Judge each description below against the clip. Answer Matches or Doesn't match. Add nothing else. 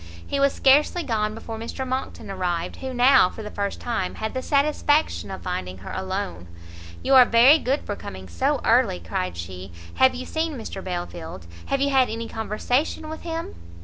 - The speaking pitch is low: Doesn't match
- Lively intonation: Matches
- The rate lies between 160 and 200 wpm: Matches